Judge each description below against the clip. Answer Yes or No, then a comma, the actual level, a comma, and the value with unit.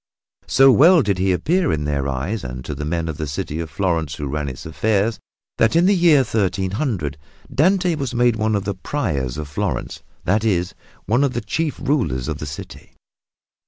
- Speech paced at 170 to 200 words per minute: Yes, average, 195 wpm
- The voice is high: No, low, 100 Hz